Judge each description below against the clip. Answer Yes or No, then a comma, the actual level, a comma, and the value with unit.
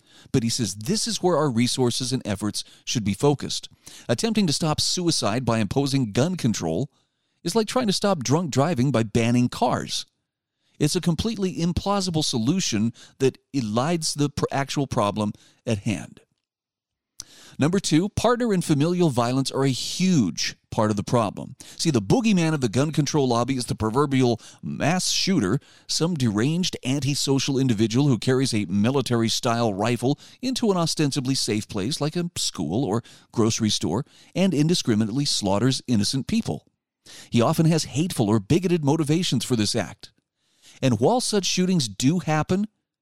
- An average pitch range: No, wide, 5.8 semitones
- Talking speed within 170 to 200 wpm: No, average, 155 wpm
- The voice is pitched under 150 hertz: Yes, low, 135 Hz